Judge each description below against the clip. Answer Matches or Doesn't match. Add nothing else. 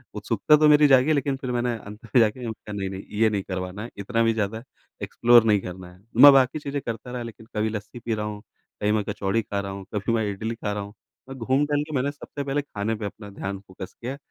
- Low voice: Matches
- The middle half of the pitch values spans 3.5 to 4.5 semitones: Matches